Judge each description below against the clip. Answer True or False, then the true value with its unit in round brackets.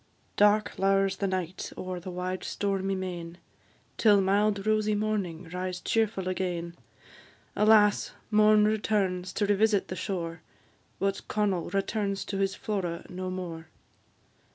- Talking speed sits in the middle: False (130 wpm)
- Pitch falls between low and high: False (195 Hz)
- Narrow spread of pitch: True (2.3 semitones)